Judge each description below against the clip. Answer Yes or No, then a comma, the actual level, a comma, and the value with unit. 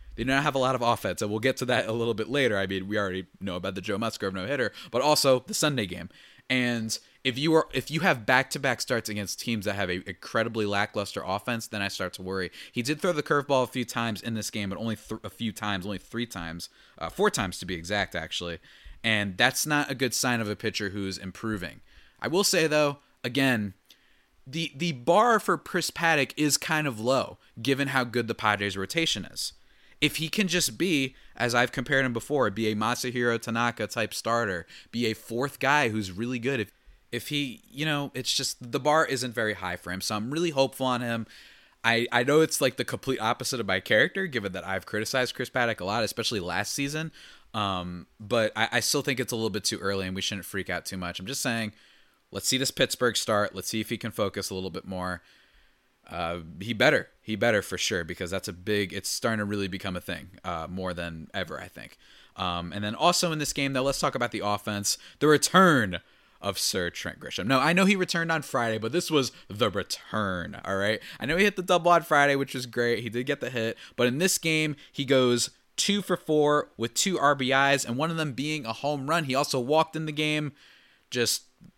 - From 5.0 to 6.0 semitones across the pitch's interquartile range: Yes, wide, 5.5 semitones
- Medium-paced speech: No, fast, 235 wpm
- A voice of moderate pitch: No, low, 120 Hz